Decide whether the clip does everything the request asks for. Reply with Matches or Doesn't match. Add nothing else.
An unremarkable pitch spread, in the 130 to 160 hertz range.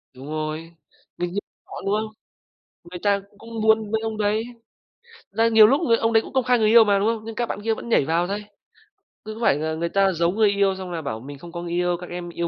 Doesn't match